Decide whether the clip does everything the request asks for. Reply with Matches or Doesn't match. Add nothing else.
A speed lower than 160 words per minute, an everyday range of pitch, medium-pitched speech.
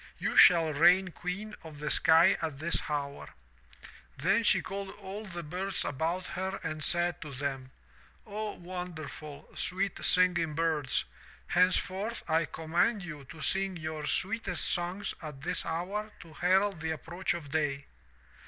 Matches